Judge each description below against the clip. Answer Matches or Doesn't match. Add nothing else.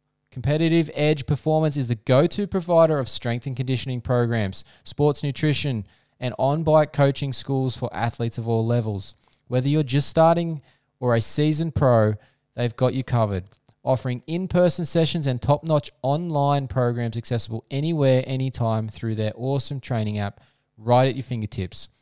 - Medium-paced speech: Matches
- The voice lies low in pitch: Matches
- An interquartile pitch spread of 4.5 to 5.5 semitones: Doesn't match